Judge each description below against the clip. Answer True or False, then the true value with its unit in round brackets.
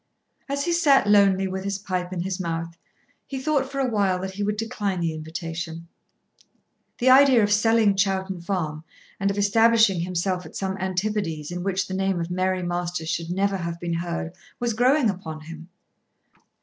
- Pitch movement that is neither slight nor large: True (3.4 semitones)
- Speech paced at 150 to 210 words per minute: True (180 wpm)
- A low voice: False (190 Hz)